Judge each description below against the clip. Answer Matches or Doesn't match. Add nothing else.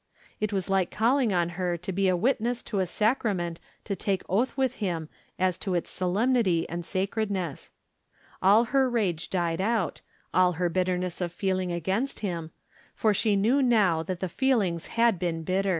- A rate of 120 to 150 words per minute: Doesn't match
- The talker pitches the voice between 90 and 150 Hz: Doesn't match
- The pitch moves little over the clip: Doesn't match